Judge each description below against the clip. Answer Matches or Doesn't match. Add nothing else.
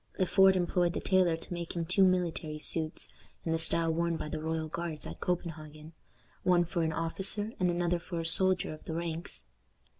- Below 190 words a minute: Doesn't match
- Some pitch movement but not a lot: Doesn't match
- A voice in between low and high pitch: Matches